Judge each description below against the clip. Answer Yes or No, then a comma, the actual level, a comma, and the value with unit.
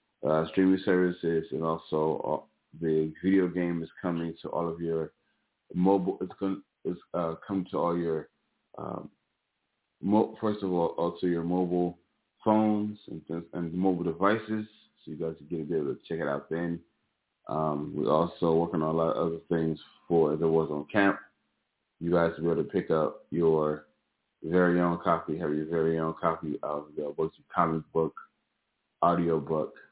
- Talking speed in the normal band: Yes, average, 180 wpm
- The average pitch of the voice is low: Yes, very low, 85 Hz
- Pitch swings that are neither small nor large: No, narrow, 2.0 semitones